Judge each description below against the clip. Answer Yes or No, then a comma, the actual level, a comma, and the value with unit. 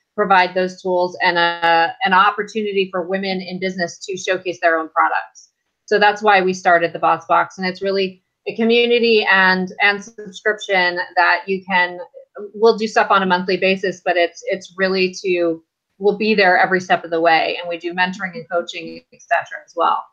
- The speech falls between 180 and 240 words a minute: Yes, average, 190 wpm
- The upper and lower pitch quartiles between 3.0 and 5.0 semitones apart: No, narrow, 2.5 semitones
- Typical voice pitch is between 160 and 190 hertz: Yes, medium, 185 Hz